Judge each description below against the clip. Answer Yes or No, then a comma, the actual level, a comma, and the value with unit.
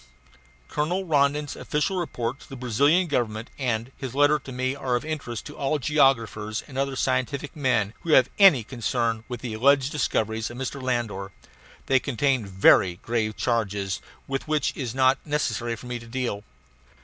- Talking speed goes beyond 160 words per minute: Yes, average, 175 wpm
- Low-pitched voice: Yes, low, 130 Hz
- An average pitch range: Yes, average, 3.6 semitones